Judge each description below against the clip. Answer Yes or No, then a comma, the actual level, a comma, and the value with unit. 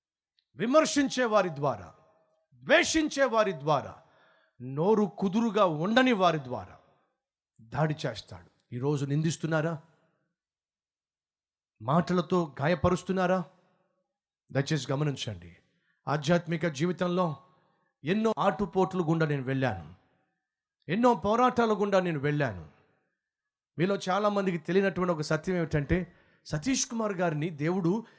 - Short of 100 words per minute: Yes, average, 90 wpm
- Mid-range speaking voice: Yes, medium, 170 Hz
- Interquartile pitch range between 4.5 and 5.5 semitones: Yes, average, 5.2 semitones